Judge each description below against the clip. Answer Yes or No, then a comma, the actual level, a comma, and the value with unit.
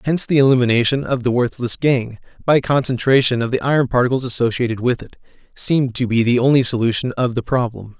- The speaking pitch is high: No, low, 125 Hz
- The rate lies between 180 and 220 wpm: Yes, average, 190 wpm